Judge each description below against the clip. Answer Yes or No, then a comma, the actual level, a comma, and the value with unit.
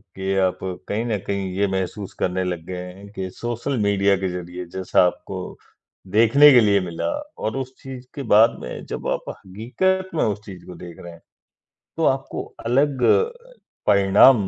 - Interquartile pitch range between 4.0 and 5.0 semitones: Yes, average, 4.4 semitones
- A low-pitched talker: Yes, low, 100 Hz